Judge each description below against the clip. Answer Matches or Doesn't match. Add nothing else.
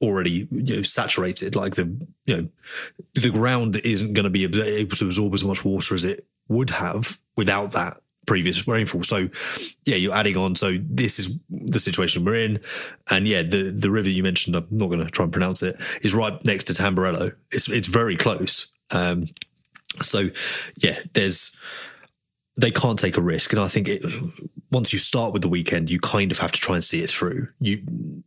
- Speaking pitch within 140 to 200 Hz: Doesn't match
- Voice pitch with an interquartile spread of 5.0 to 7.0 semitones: Doesn't match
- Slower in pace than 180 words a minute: Doesn't match